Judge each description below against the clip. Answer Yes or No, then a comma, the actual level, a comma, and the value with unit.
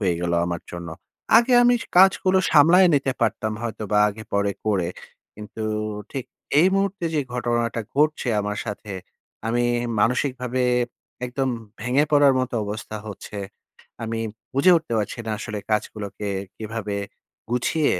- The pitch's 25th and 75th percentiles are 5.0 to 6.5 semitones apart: Yes, average, 5.3 semitones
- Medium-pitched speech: No, low, 120 Hz